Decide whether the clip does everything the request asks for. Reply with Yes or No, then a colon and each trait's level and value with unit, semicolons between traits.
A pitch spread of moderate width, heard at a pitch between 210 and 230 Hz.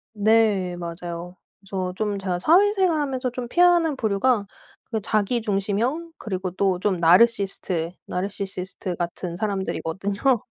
No: average, 4.8 semitones; high, 200 Hz